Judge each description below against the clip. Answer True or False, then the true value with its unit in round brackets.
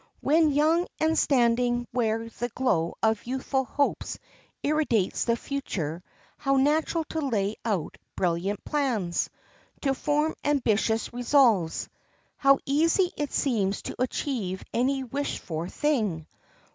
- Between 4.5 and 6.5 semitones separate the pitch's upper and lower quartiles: True (5.3 semitones)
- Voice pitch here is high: True (250 Hz)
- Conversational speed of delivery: False (120 wpm)